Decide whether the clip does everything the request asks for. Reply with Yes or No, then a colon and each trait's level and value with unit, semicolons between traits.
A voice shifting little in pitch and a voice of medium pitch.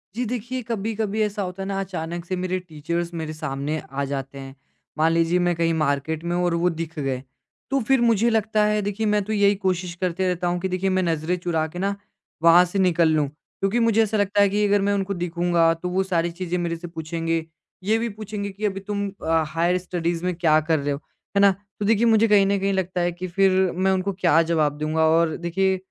No: average, 3.3 semitones; medium, 180 Hz